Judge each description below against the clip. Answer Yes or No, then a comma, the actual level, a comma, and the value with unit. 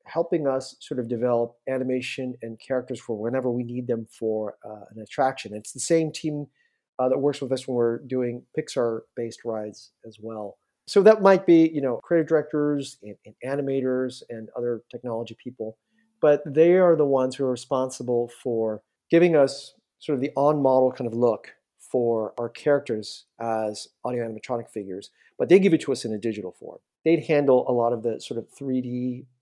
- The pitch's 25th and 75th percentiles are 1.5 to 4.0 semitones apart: Yes, average, 3.3 semitones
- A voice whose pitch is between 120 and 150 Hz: Yes, low, 125 Hz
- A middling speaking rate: Yes, average, 190 wpm